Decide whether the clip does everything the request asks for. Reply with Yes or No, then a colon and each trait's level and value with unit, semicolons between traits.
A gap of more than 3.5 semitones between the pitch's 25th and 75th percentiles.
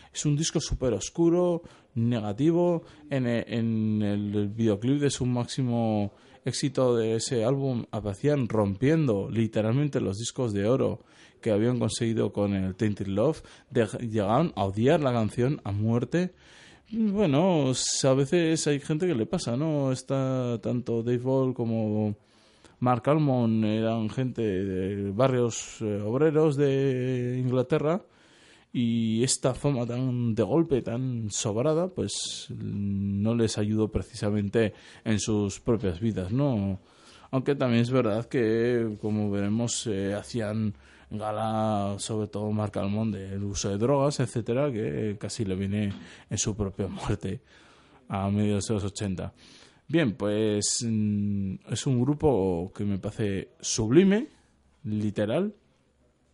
Yes: average, 4.1 semitones